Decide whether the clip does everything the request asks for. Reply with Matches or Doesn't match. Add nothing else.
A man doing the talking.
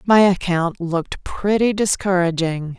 Doesn't match